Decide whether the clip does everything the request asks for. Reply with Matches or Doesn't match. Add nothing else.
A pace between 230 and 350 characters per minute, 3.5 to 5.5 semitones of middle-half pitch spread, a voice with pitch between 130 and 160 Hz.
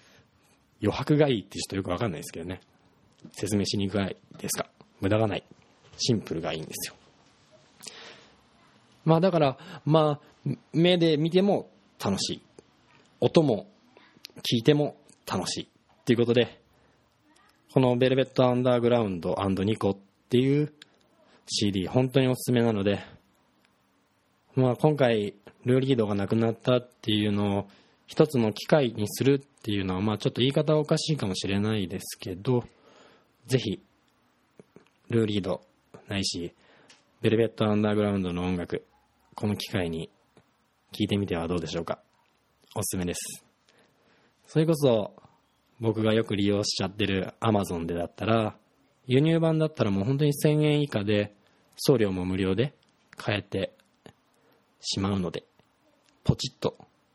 Doesn't match